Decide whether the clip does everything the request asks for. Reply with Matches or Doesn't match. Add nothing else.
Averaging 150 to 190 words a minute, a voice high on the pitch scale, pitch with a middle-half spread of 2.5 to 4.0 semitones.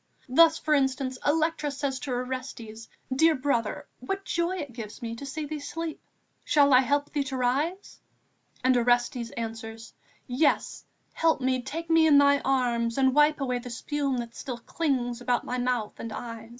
Matches